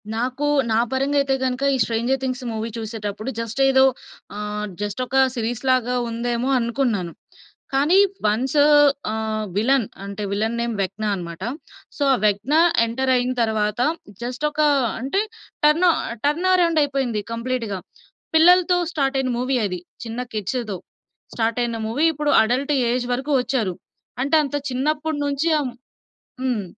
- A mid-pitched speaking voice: No, very high, 250 Hz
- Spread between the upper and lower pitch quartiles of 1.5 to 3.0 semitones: No, average, 3.8 semitones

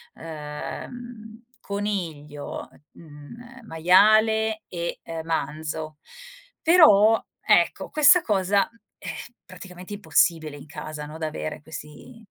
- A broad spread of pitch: Yes, wide, 5.9 semitones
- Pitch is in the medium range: Yes, medium, 180 Hz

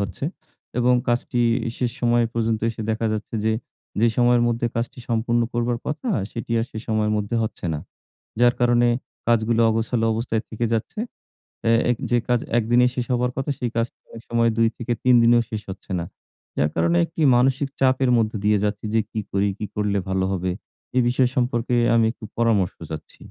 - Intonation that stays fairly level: Yes, narrow, 1.8 semitones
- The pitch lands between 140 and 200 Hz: No, low, 115 Hz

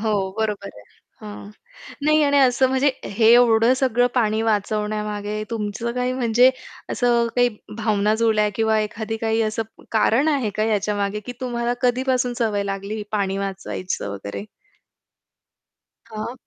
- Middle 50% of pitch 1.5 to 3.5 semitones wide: Yes, average, 2.7 semitones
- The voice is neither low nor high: No, high, 220 Hz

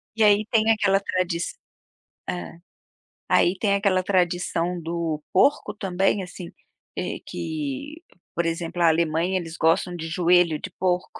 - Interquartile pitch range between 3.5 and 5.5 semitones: No, average, 2.8 semitones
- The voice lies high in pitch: No, medium, 180 Hz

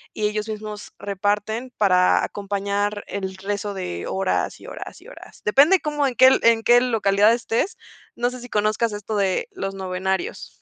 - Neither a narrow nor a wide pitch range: Yes, average, 3.1 semitones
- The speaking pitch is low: No, high, 210 Hz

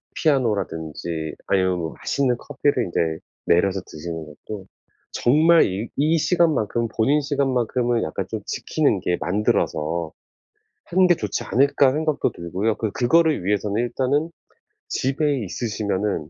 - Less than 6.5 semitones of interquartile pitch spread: No, wide, 7.4 semitones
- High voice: No, low, 115 Hz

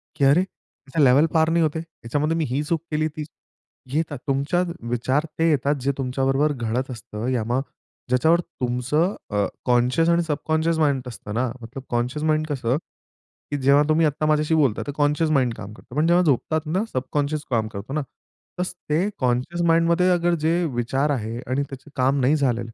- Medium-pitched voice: Yes, medium, 145 Hz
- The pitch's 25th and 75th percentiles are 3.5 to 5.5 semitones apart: Yes, average, 3.9 semitones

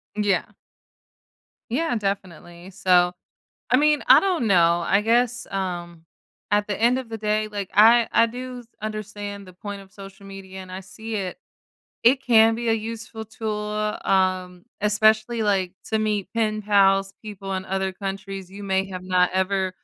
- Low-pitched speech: No, high, 205 Hz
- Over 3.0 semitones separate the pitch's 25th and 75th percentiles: No, narrow, 2.6 semitones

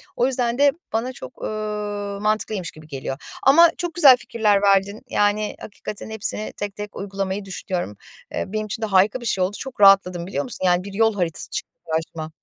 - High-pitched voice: Yes, high, 205 Hz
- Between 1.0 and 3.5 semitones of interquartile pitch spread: Yes, narrow, 2.6 semitones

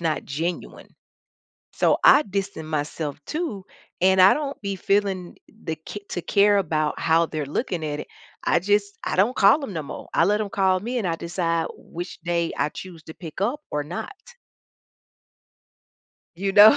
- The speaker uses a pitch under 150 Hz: No, medium, 185 Hz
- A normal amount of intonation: Yes, average, 3.8 semitones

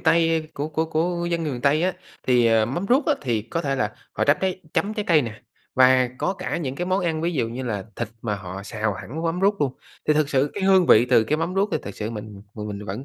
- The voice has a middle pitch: Yes, medium, 145 Hz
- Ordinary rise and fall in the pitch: No, wide, 7.1 semitones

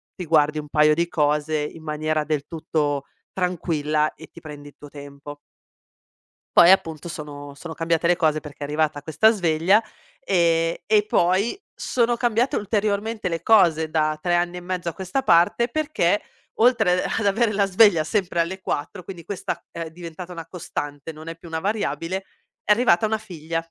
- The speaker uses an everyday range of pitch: Yes, average, 4.1 semitones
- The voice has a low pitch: No, medium, 170 Hz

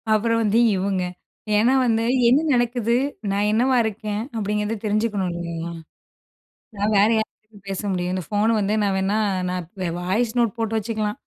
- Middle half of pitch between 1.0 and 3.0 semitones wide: Yes, narrow, 2.4 semitones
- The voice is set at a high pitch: Yes, high, 210 Hz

